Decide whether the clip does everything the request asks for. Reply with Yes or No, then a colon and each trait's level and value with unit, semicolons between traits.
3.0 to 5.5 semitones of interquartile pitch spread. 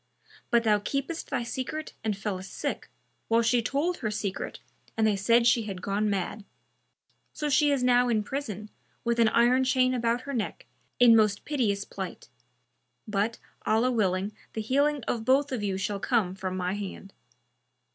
Yes: average, 3.9 semitones